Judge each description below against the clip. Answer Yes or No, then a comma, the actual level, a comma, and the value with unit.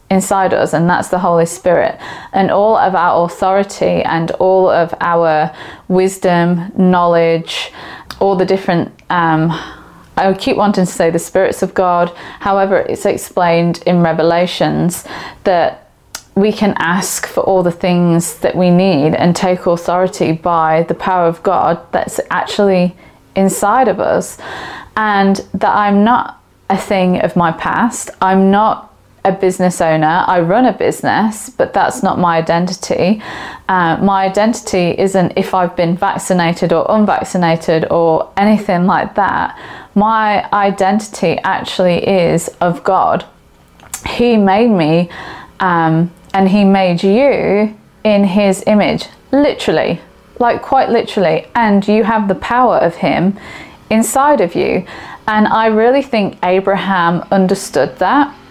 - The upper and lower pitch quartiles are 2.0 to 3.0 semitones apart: Yes, average, 2.7 semitones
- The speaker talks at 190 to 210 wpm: No, average, 140 wpm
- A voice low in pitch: No, high, 190 Hz